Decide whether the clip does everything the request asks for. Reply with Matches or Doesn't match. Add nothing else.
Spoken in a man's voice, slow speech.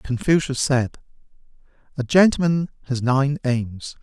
Matches